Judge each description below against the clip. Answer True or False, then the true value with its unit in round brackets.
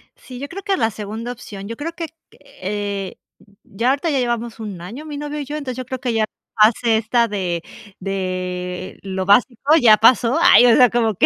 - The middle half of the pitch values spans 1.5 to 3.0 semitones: False (4.5 semitones)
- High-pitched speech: True (230 Hz)